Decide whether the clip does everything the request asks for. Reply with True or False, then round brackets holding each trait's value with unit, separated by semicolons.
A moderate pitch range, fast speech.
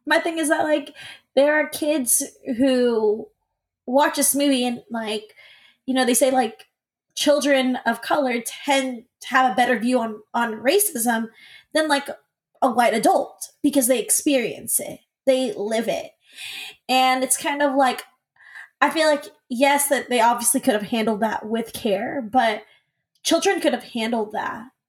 False (3.5 semitones; 160 wpm)